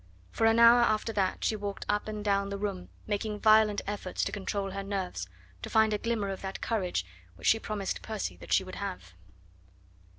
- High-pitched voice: Yes, high, 205 Hz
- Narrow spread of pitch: Yes, narrow, 1.8 semitones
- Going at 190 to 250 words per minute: Yes, average, 200 wpm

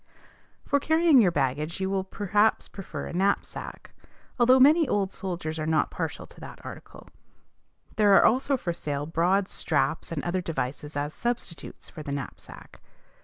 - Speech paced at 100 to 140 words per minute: No, average, 160 wpm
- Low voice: No, medium, 185 Hz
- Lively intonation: Yes, wide, 6.1 semitones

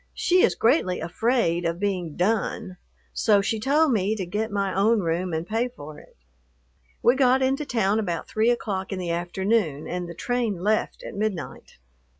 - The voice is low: No, high, 205 Hz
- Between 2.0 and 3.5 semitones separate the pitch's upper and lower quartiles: No, average, 4.6 semitones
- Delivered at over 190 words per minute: No, average, 175 wpm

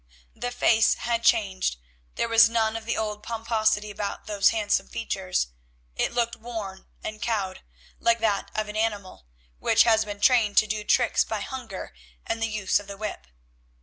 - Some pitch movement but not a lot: No, narrow, 2.1 semitones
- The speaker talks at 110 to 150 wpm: No, average, 175 wpm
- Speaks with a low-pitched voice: No, high, 215 Hz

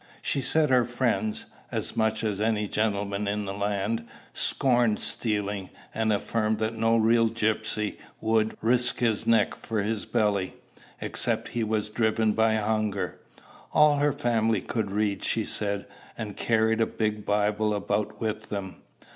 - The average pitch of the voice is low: Yes, low, 110 Hz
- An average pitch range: No, narrow, 1.5 semitones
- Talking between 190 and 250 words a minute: No, average, 150 wpm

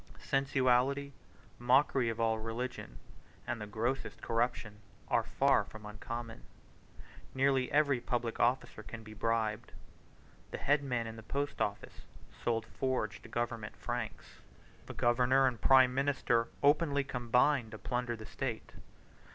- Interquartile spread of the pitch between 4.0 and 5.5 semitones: No, average, 2.9 semitones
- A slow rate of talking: Yes, slow, 130 wpm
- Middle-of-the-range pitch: No, low, 120 Hz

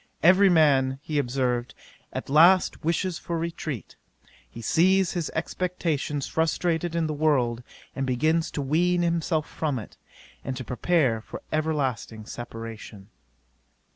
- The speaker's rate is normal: No, slow, 130 wpm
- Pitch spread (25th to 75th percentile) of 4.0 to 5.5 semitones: Yes, average, 4.7 semitones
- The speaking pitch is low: No, medium, 155 Hz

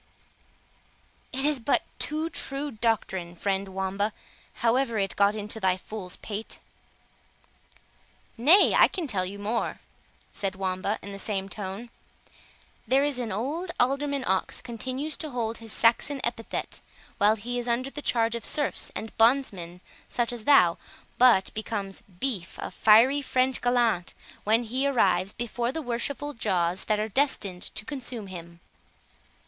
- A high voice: Yes, high, 225 Hz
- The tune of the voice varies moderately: Yes, average, 4.7 semitones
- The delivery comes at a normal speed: Yes, average, 145 wpm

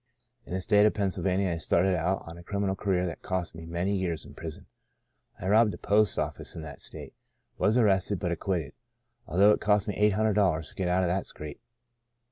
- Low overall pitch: Yes, very low, 95 Hz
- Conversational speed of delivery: No, fast, 215 wpm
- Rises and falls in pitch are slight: No, average, 3.0 semitones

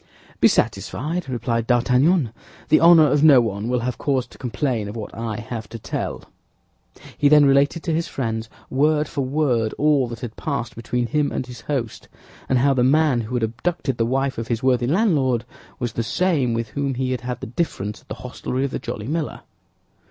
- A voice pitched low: Yes, low, 125 Hz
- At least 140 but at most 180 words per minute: No, fast, 205 wpm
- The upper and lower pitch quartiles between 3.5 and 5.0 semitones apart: Yes, average, 3.8 semitones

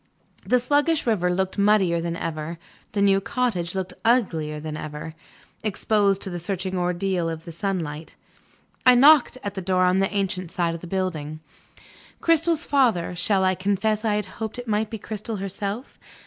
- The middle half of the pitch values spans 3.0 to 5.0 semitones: Yes, average, 3.8 semitones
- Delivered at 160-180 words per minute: Yes, average, 175 wpm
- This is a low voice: No, high, 190 Hz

